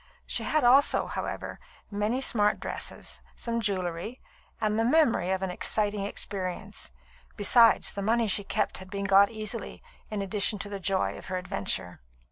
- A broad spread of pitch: No, average, 2.8 semitones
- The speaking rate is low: No, average, 160 wpm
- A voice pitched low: No, high, 205 Hz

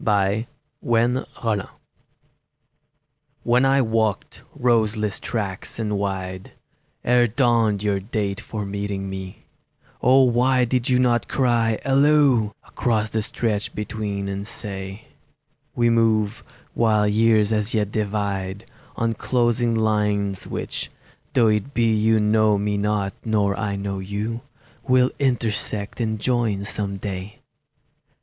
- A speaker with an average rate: No, slow, 120 wpm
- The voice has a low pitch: Yes, low, 110 Hz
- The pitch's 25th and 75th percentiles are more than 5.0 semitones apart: No, narrow, 2.6 semitones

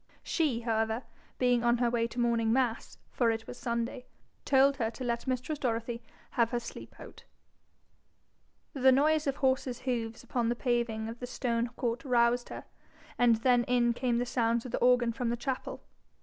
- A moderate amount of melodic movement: No, narrow, 1.5 semitones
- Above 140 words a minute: Yes, average, 180 wpm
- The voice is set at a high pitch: Yes, high, 240 Hz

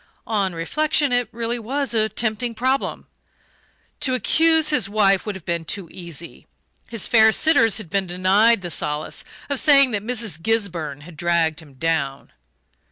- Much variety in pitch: Yes, wide, 6.0 semitones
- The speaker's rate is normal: Yes, average, 160 wpm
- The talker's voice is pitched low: No, high, 210 Hz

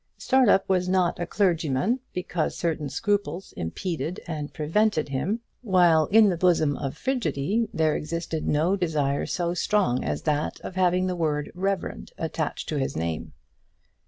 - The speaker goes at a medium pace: Yes, average, 150 wpm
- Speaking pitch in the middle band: Yes, medium, 170 Hz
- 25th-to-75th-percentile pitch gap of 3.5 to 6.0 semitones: Yes, average, 4.0 semitones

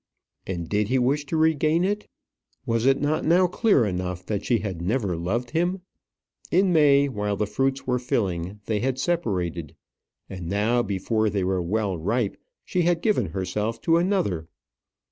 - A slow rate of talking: No, average, 165 wpm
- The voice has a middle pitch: No, low, 115 Hz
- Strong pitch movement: Yes, wide, 8.1 semitones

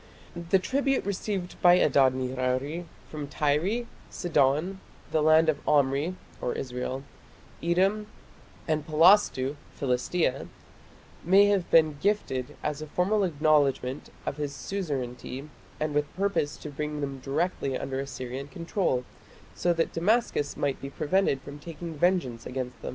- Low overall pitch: No, medium, 150 Hz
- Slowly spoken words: Yes, slow, 130 wpm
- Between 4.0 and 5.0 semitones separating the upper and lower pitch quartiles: Yes, average, 4.7 semitones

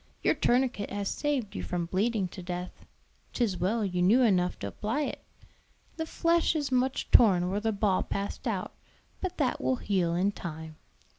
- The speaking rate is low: No, average, 175 wpm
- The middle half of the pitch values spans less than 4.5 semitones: No, wide, 5.6 semitones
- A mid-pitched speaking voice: No, high, 205 Hz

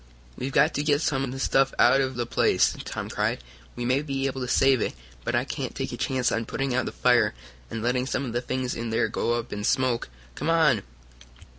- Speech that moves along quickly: Yes, fast, 240 wpm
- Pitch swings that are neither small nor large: No, narrow, 2.1 semitones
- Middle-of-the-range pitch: No, low, 130 Hz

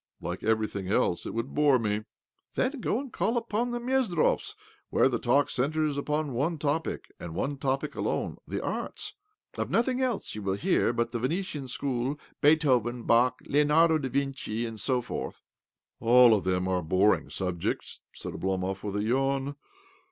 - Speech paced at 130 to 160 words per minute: No, average, 175 wpm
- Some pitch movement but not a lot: No, wide, 6.0 semitones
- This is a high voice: No, low, 130 Hz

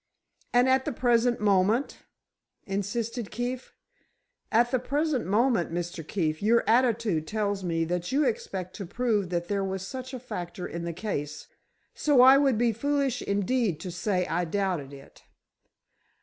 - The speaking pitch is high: Yes, high, 210 Hz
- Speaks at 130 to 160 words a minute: Yes, average, 155 wpm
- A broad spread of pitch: Yes, wide, 5.7 semitones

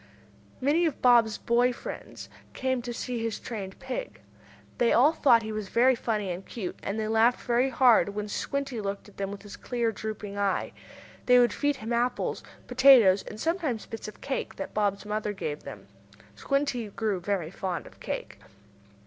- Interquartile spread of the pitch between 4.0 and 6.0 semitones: No, average, 3.6 semitones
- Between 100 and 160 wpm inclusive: No, average, 180 wpm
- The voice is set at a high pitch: Yes, high, 225 Hz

